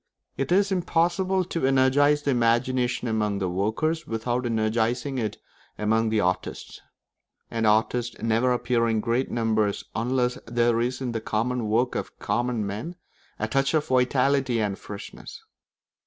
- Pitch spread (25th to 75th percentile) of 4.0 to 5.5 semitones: No, average, 2.9 semitones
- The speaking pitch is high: No, low, 120 Hz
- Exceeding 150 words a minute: No, average, 145 wpm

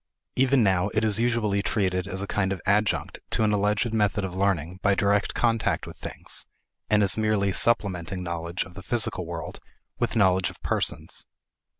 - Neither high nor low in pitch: No, low, 100 Hz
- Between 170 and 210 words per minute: Yes, average, 180 wpm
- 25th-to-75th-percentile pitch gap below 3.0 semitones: Yes, narrow, 2.4 semitones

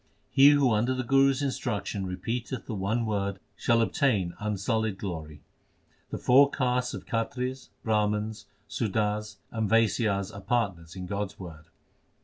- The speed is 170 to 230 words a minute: No, average, 145 wpm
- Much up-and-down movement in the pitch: No, average, 3.9 semitones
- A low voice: Yes, low, 110 Hz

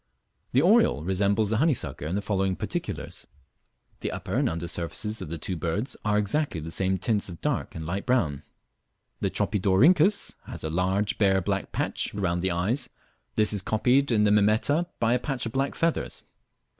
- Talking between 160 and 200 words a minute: Yes, average, 185 wpm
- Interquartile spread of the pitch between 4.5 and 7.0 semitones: Yes, average, 5.1 semitones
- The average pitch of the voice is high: No, low, 105 Hz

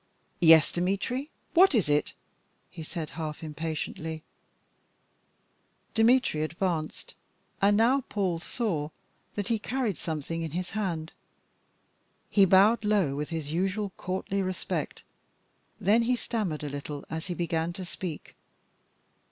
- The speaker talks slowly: Yes, slow, 125 wpm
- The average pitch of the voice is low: No, medium, 180 Hz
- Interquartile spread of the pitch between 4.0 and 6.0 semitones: Yes, average, 4.7 semitones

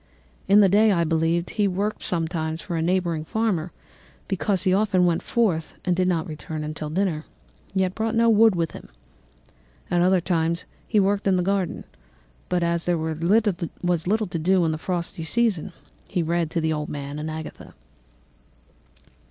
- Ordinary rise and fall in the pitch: Yes, average, 3.3 semitones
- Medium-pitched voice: Yes, medium, 175 Hz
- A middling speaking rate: Yes, average, 175 wpm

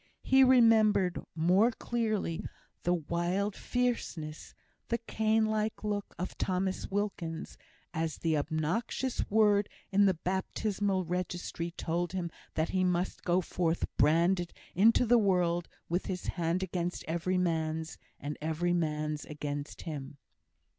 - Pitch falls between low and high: Yes, medium, 180 Hz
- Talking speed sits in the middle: No, slow, 125 wpm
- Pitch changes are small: No, average, 3.8 semitones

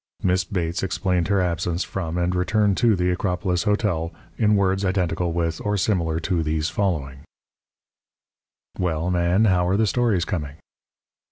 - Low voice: Yes, very low, 90 Hz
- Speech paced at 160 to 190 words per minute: No, average, 150 wpm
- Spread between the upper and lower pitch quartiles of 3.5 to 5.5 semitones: No, average, 2.7 semitones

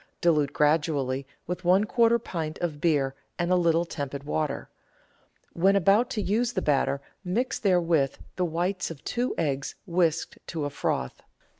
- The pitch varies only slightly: No, average, 4.3 semitones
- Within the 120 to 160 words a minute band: Yes, average, 155 wpm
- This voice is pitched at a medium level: Yes, medium, 170 Hz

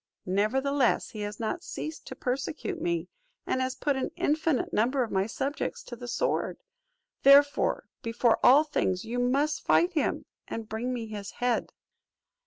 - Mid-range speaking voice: No, very high, 255 Hz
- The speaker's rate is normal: Yes, average, 165 wpm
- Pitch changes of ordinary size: Yes, average, 4.2 semitones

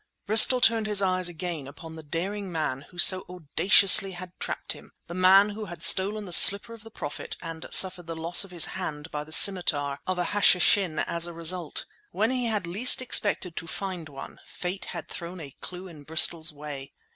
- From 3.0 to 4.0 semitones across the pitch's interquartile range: Yes, average, 3.6 semitones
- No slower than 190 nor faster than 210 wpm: Yes, average, 195 wpm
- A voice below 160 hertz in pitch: No, medium, 180 Hz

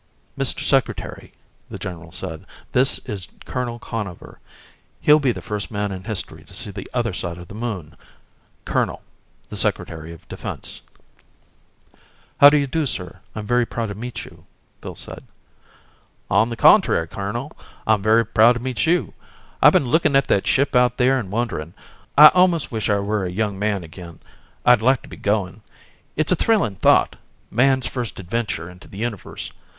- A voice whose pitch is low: Yes, low, 110 Hz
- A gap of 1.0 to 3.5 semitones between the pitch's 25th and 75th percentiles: No, average, 4.7 semitones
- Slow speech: No, average, 175 wpm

